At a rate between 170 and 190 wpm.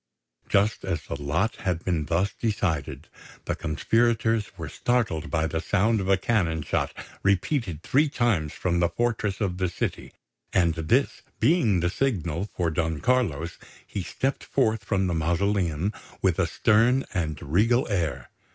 No: average, 155 wpm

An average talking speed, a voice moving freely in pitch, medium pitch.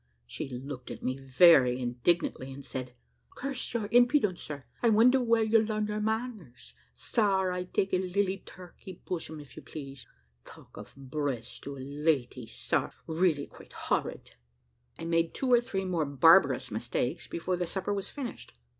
Yes: average, 165 wpm; wide, 7.1 semitones; medium, 165 Hz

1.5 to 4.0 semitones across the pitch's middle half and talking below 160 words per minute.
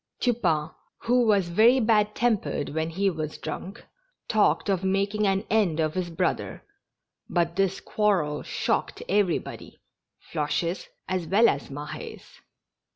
No: average, 4.6 semitones; slow, 135 wpm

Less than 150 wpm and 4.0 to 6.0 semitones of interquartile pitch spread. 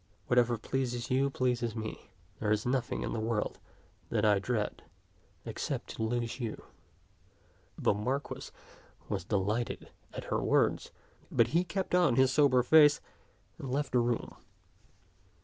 No: average, 140 wpm; average, 3.1 semitones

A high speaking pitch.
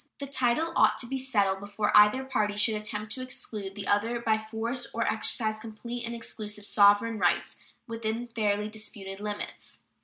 Yes: high, 220 Hz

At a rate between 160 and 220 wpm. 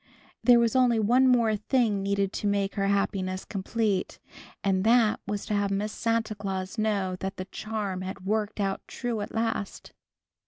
Yes: average, 170 wpm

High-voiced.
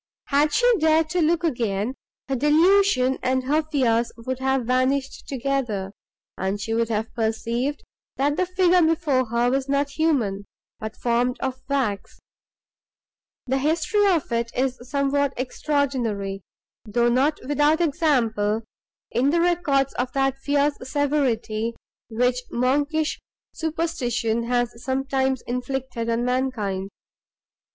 Yes: very high, 265 Hz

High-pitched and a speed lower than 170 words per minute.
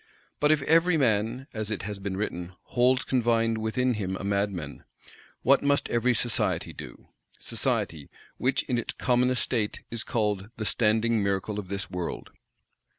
No: low, 110 Hz; average, 155 wpm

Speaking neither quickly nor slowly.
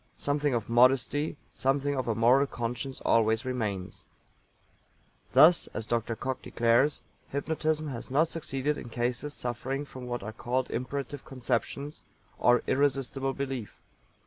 No: slow, 130 wpm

